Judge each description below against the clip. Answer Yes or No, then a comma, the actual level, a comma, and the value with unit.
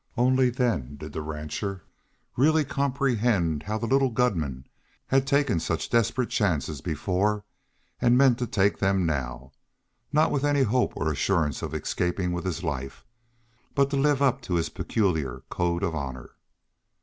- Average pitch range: No, wide, 8.4 semitones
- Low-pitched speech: Yes, low, 100 Hz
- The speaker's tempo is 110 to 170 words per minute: Yes, average, 155 wpm